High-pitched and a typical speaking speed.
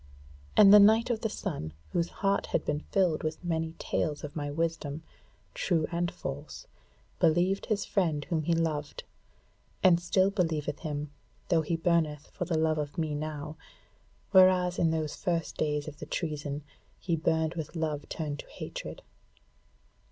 No: medium, 160 Hz; average, 160 wpm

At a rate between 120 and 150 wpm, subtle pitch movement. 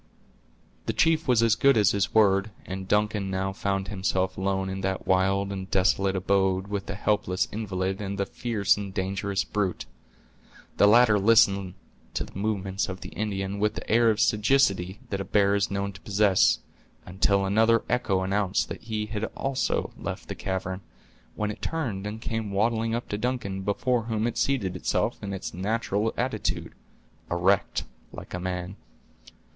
No: average, 170 wpm; narrow, 2.1 semitones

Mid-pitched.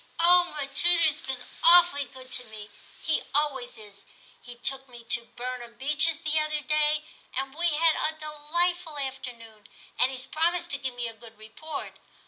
No: very high, 280 Hz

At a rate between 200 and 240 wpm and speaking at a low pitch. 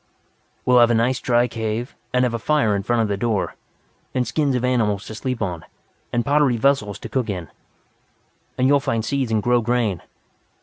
Yes: fast, 205 wpm; low, 120 Hz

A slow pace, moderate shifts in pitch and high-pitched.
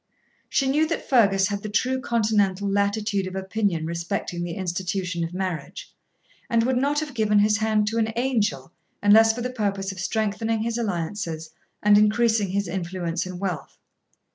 No: average, 165 wpm; average, 3.3 semitones; high, 205 Hz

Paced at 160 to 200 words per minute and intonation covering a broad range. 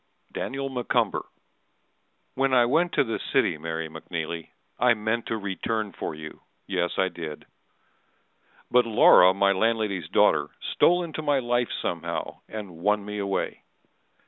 No: average, 140 wpm; wide, 5.8 semitones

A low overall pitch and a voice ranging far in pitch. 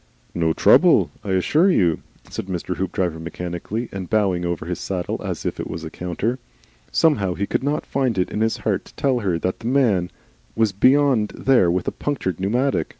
Yes: very low, 95 Hz; wide, 5.8 semitones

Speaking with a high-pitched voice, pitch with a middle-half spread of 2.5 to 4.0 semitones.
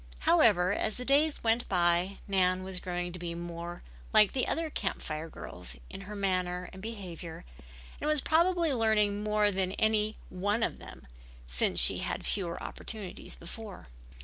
Yes: high, 195 Hz; average, 3.7 semitones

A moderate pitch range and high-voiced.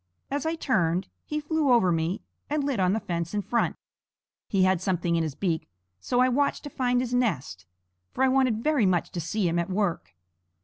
No: wide, 7.0 semitones; high, 205 Hz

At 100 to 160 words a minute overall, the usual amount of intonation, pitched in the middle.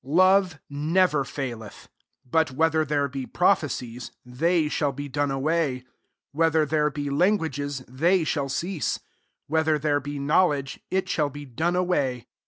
Yes: average, 150 wpm; average, 3.1 semitones; medium, 145 Hz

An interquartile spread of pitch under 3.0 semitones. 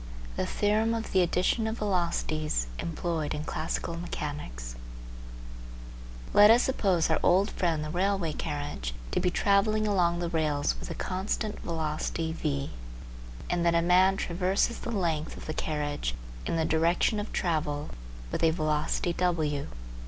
No: average, 3.8 semitones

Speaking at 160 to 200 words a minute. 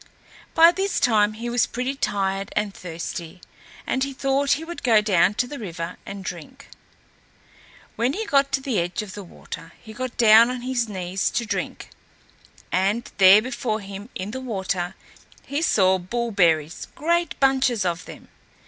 Yes: average, 165 wpm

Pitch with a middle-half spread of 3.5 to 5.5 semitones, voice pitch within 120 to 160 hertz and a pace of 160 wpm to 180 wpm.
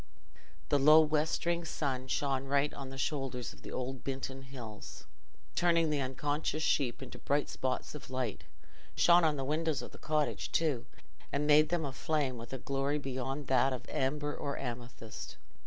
No: narrow, 2.6 semitones; medium, 140 Hz; average, 170 wpm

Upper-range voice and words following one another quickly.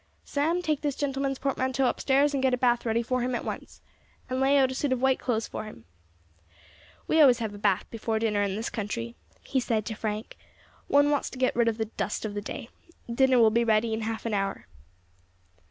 Yes: high, 240 Hz; fast, 220 wpm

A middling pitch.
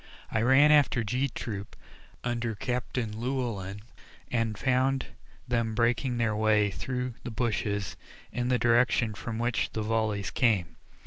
No: low, 115 Hz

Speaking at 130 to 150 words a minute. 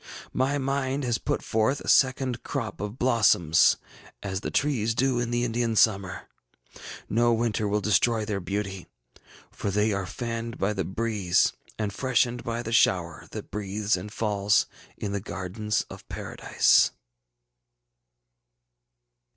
Yes: average, 140 wpm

